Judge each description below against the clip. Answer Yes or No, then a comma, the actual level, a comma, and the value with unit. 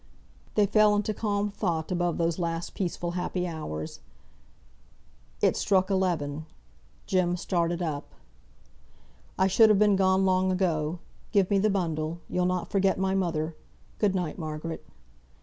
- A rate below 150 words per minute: Yes, average, 140 wpm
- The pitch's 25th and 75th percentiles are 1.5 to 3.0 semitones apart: Yes, average, 2.7 semitones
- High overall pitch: No, medium, 180 Hz